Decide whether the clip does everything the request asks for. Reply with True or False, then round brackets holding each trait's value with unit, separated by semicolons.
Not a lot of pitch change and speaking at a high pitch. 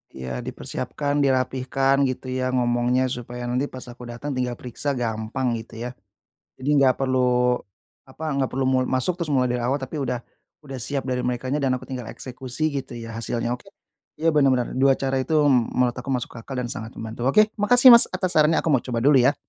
False (2.2 semitones; 130 Hz)